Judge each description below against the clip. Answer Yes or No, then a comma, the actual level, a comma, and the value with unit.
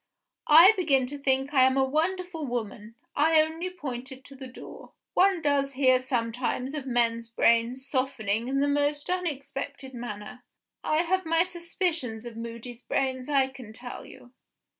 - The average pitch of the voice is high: Yes, very high, 265 Hz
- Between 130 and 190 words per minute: Yes, average, 160 wpm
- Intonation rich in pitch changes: No, average, 4.1 semitones